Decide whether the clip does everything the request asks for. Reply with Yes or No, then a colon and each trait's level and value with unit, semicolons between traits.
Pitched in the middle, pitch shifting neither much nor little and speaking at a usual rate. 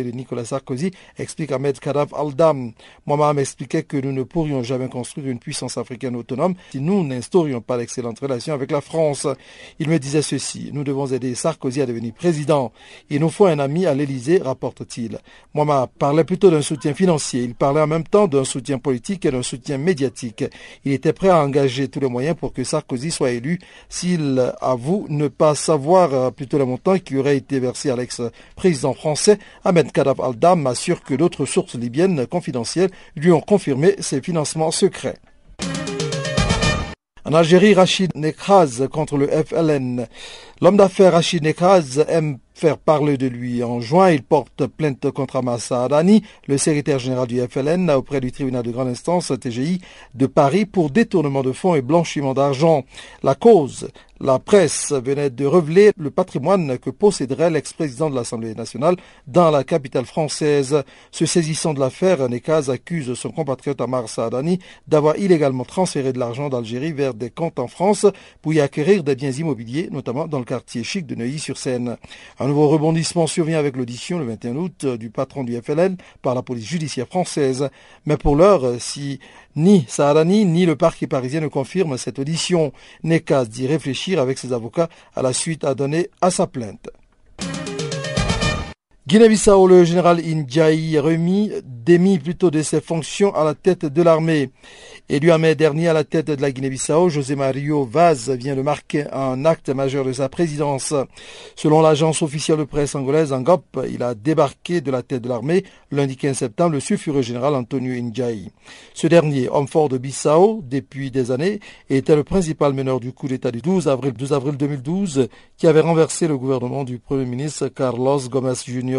Yes: medium, 145 Hz; average, 4.0 semitones; average, 175 wpm